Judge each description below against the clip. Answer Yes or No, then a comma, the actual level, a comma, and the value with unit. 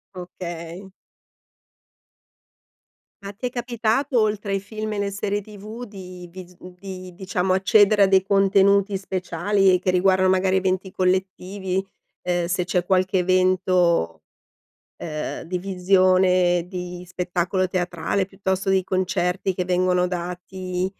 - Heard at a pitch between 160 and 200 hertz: Yes, medium, 185 Hz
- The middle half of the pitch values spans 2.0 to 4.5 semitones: No, narrow, 1.5 semitones